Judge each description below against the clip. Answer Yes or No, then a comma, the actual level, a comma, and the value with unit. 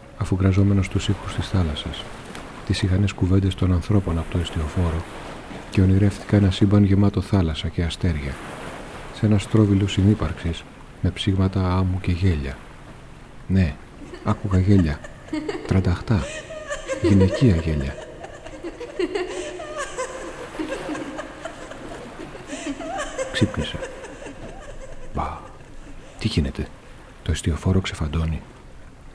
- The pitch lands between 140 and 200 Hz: No, very low, 95 Hz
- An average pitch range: Yes, average, 4.2 semitones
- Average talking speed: No, slow, 90 wpm